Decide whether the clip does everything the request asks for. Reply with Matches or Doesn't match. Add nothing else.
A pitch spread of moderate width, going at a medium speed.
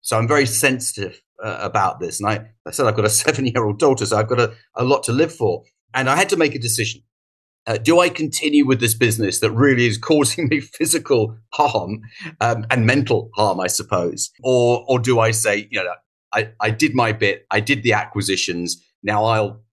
Doesn't match